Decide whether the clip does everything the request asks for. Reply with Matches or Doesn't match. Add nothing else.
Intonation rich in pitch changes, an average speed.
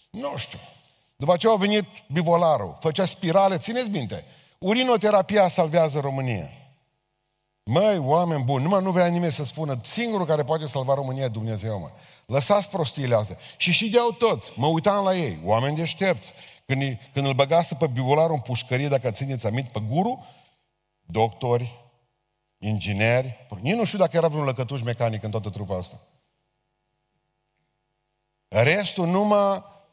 Matches